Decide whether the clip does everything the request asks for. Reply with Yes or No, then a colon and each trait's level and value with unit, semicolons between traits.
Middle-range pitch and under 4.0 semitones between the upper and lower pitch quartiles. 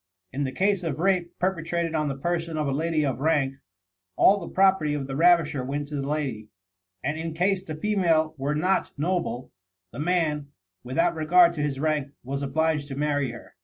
Yes: medium, 155 Hz; average, 3.3 semitones